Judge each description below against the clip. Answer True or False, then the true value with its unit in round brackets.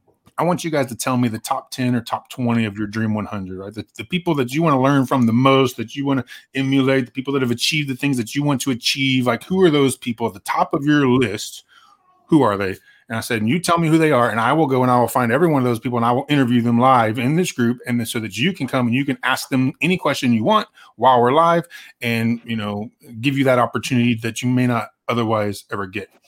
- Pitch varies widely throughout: False (3.3 semitones)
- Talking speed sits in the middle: False (285 wpm)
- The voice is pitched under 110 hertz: False (130 Hz)